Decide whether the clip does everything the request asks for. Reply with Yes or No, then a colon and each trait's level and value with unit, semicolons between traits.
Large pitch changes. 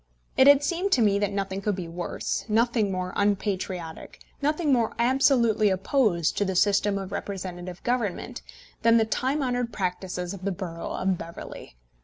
No: average, 4.5 semitones